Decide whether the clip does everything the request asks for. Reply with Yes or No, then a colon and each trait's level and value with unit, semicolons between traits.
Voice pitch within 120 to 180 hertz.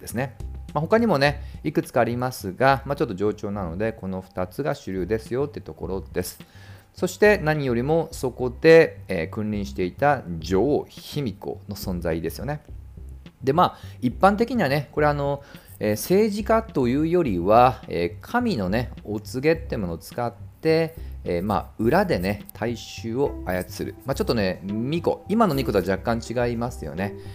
No: low, 110 Hz